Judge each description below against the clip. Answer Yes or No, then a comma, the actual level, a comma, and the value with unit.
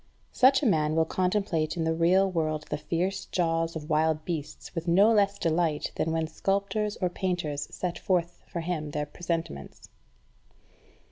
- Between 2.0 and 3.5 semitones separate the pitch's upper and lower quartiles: Yes, average, 2.9 semitones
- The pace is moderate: Yes, average, 160 wpm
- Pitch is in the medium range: Yes, medium, 170 Hz